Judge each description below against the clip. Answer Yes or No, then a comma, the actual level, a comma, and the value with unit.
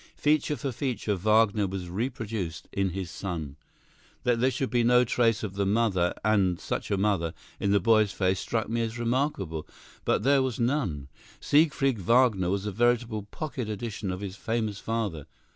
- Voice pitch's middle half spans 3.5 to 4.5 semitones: Yes, average, 3.9 semitones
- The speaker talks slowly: No, average, 175 wpm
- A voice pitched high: No, low, 110 Hz